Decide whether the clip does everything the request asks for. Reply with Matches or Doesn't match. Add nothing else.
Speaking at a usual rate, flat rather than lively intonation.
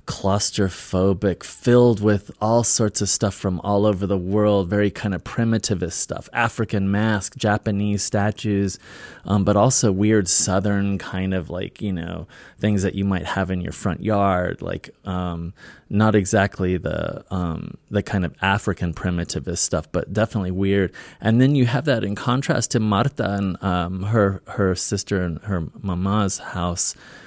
Matches